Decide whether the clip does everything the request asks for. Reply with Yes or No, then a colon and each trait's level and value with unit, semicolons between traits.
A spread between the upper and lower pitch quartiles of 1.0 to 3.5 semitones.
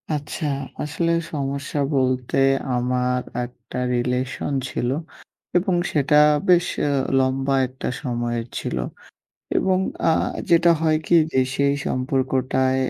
Yes: average, 2.8 semitones